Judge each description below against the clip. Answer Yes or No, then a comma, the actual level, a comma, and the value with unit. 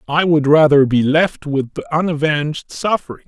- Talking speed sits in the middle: Yes, average, 165 wpm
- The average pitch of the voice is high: No, medium, 150 Hz